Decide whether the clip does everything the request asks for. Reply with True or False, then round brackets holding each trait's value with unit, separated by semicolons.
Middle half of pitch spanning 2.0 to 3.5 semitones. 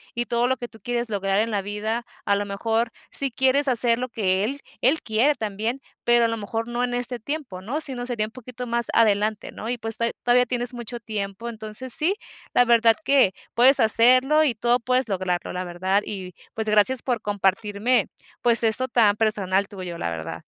True (3.2 semitones)